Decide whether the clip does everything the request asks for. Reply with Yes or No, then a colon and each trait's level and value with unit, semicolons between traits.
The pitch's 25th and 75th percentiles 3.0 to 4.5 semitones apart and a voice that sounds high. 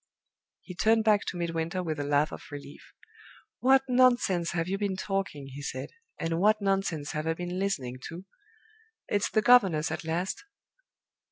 No: average, 4.2 semitones; medium, 180 Hz